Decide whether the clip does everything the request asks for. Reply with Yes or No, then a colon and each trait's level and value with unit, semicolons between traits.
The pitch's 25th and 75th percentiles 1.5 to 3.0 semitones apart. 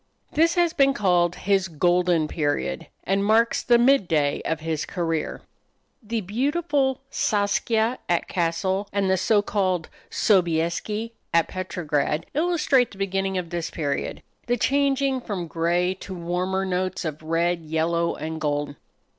No: average, 5.0 semitones